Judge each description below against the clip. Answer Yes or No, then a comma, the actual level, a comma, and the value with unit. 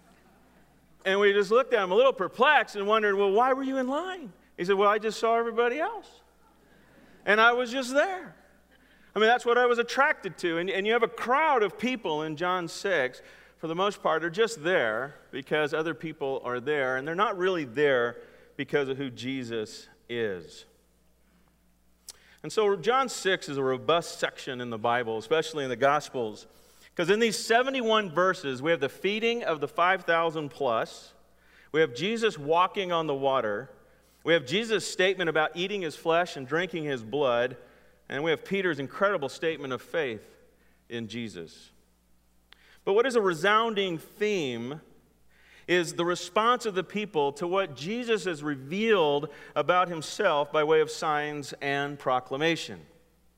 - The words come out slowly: No, average, 170 wpm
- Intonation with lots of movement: Yes, wide, 6.6 semitones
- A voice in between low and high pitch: Yes, medium, 170 Hz